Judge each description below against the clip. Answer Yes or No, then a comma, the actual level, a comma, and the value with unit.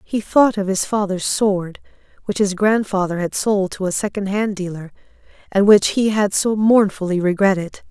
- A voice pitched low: No, high, 200 Hz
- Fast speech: No, average, 165 wpm